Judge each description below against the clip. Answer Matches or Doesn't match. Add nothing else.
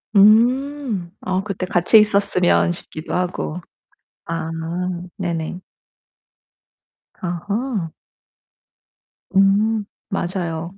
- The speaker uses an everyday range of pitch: Matches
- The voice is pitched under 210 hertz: Matches